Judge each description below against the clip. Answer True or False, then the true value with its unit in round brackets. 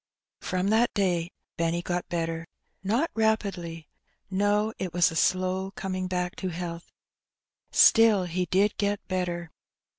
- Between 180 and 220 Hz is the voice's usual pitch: True (185 Hz)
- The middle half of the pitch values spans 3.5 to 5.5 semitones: False (2.7 semitones)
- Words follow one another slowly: True (130 wpm)